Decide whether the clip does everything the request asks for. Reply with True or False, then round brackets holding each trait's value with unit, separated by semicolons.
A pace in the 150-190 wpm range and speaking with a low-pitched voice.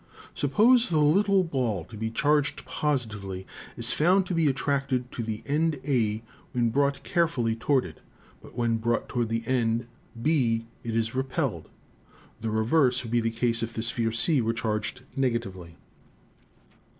True (160 wpm; 120 Hz)